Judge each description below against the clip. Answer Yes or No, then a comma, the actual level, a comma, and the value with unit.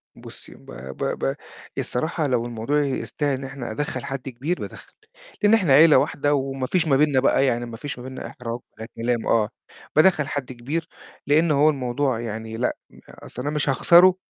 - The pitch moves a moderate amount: Yes, average, 3.6 semitones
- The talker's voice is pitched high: No, low, 135 Hz